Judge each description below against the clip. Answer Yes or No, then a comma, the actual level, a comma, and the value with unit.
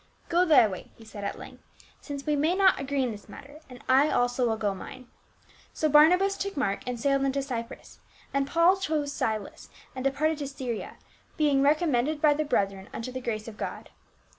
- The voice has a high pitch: Yes, very high, 275 Hz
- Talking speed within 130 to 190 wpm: No, average, 200 wpm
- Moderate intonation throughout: Yes, average, 4.2 semitones